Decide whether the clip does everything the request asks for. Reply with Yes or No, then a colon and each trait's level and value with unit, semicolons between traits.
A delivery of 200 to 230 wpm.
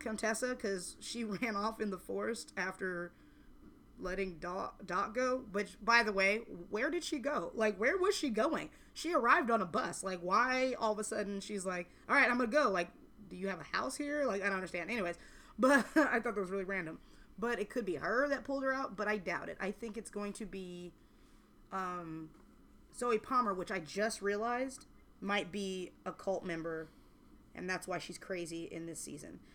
Yes: fast, 205 wpm